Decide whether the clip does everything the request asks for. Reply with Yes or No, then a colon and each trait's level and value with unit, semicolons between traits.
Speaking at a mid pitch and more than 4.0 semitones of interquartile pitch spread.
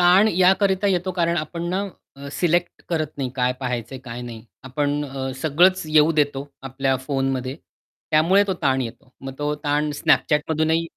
Yes: medium, 150 Hz; average, 4.5 semitones